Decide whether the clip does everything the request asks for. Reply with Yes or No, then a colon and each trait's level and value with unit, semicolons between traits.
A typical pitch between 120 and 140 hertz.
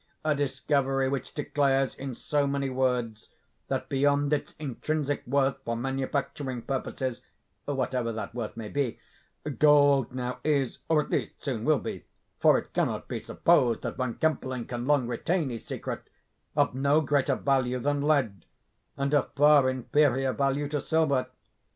Yes: low, 135 Hz